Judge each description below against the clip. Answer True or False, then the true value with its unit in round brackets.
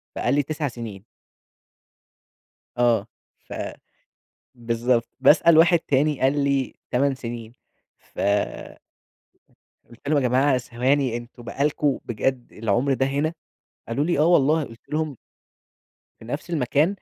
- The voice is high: False (135 Hz)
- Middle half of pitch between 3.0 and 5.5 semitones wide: True (3.6 semitones)